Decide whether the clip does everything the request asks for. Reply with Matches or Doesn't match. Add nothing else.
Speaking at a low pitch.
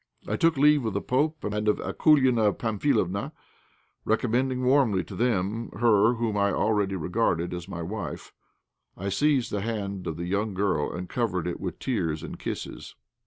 Matches